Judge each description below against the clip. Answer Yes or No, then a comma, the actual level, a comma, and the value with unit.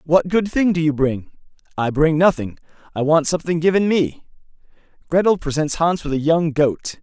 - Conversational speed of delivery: Yes, average, 180 wpm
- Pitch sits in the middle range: Yes, medium, 160 Hz